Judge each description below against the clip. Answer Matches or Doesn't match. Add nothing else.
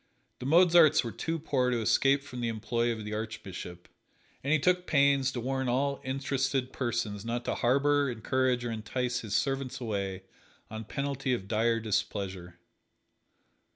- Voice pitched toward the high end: Doesn't match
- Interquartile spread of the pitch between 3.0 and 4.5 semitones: Matches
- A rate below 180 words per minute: Matches